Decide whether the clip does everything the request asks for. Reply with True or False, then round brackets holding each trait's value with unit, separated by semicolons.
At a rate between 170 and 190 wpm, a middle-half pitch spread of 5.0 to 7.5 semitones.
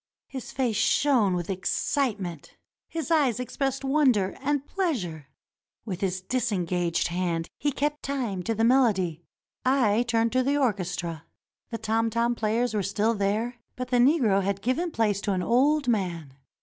False (155 wpm; 5.6 semitones)